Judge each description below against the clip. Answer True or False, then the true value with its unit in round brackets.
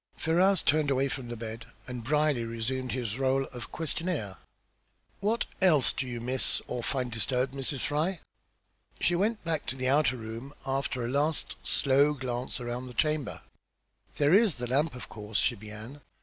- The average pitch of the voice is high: False (130 Hz)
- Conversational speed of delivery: True (170 wpm)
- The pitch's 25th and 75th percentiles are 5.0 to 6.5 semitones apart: False (3.8 semitones)